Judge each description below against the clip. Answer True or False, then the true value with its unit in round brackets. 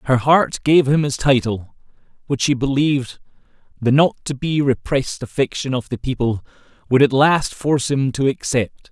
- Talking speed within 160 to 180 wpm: True (170 wpm)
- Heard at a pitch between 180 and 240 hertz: False (135 Hz)